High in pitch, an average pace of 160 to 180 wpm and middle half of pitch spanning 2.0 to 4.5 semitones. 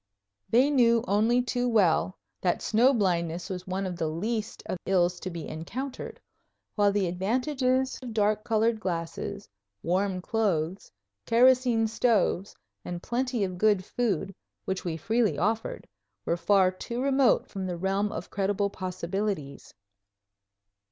No: high, 205 Hz; average, 140 wpm; average, 4.2 semitones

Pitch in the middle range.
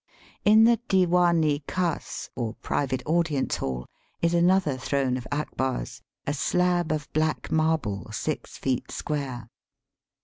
Yes: medium, 150 Hz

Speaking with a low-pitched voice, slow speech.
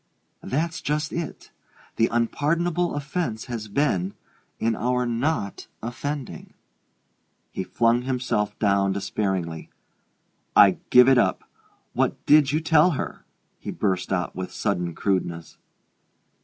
Yes: low, 120 Hz; slow, 115 wpm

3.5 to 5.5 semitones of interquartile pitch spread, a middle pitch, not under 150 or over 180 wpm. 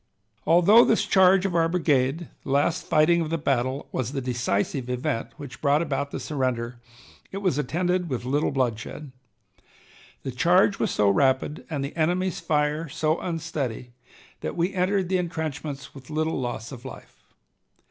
Yes: average, 4.6 semitones; medium, 150 Hz; average, 160 wpm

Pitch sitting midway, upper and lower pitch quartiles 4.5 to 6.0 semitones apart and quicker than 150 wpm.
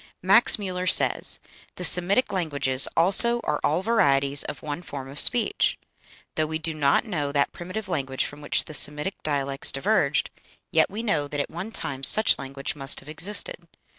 Yes: medium, 155 Hz; average, 5.2 semitones; average, 175 wpm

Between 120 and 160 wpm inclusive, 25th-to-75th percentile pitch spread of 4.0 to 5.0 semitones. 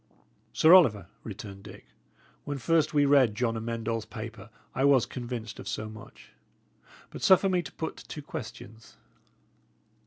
Yes: average, 150 wpm; average, 4.6 semitones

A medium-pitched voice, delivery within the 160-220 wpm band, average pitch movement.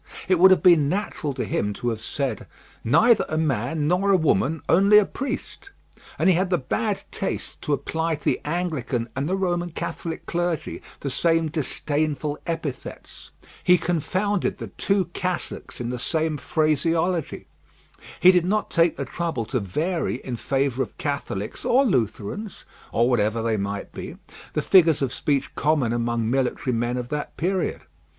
No: medium, 155 Hz; average, 165 wpm; wide, 6.0 semitones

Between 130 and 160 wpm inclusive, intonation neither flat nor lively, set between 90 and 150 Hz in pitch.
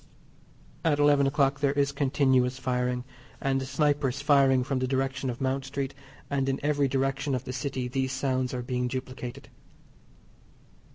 No: average, 155 wpm; narrow, 1.5 semitones; low, 135 Hz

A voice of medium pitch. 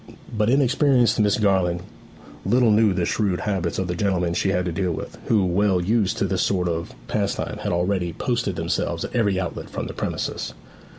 No: very low, 95 Hz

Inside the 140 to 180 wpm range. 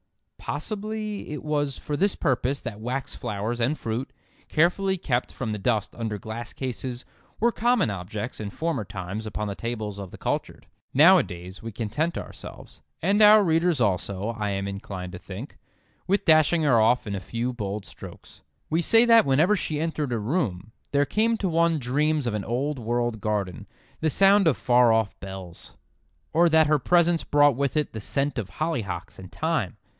Yes: average, 175 wpm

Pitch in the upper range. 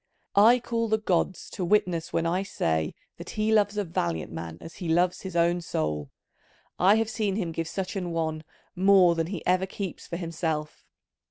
No: medium, 175 Hz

